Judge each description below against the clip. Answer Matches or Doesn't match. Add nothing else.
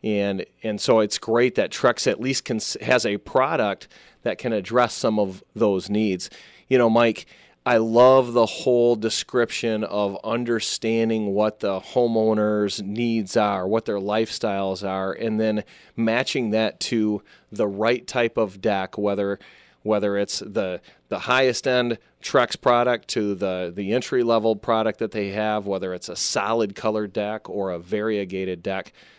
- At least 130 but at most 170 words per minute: Matches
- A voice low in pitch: Matches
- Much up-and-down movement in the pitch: Doesn't match